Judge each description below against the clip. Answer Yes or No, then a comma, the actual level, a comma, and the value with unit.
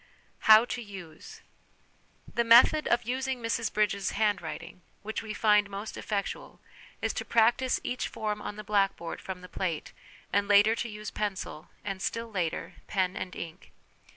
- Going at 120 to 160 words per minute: Yes, average, 155 wpm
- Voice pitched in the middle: No, high, 210 Hz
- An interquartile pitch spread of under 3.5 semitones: Yes, average, 2.7 semitones